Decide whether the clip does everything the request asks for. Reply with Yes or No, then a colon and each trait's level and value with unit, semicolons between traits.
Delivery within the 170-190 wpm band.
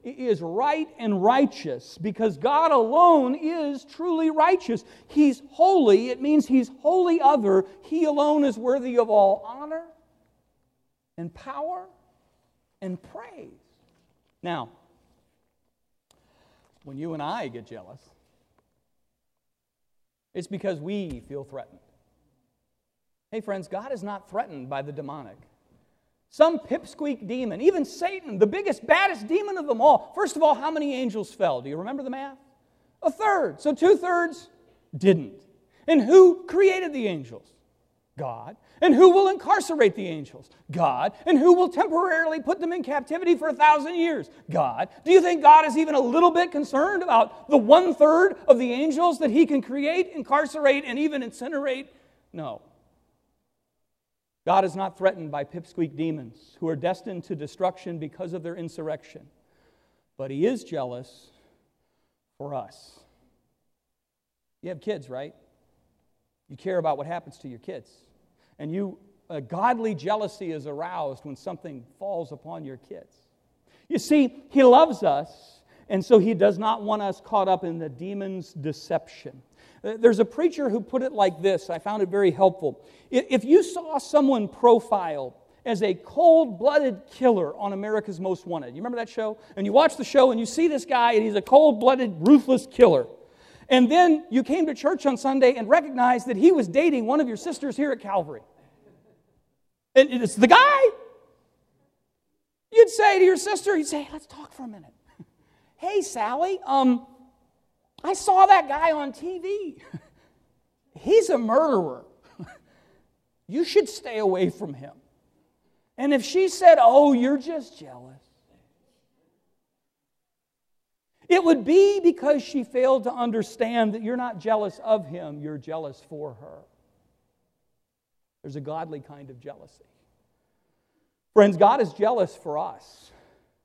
No: average, 150 wpm